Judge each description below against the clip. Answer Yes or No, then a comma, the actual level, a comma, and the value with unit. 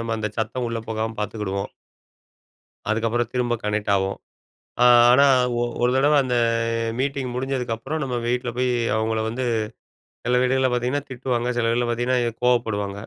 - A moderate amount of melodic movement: No, narrow, 2.3 semitones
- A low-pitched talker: Yes, low, 120 Hz